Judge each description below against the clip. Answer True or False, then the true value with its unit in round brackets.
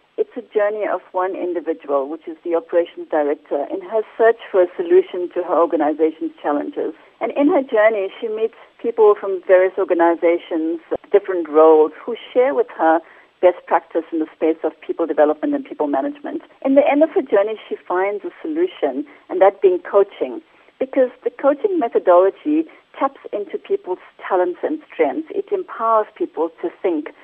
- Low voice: False (215 Hz)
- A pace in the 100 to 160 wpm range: False (170 wpm)